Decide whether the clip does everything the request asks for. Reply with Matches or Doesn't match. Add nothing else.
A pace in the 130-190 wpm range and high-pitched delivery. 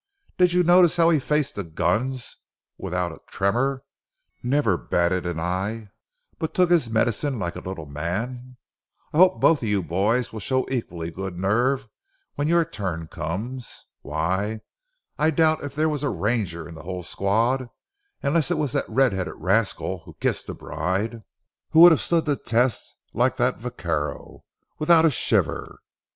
Doesn't match